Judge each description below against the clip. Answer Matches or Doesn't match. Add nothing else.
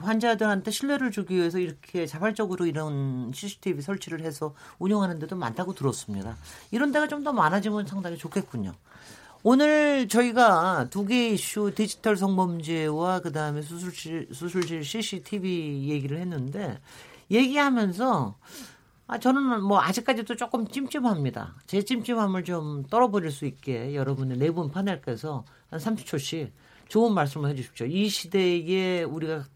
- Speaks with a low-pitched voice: Doesn't match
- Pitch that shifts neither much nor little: Doesn't match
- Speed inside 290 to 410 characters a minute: Matches